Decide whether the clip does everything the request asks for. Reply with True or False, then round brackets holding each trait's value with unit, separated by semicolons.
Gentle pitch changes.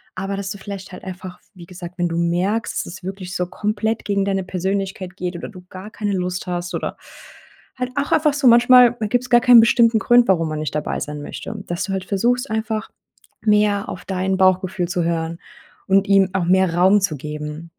False (3.1 semitones)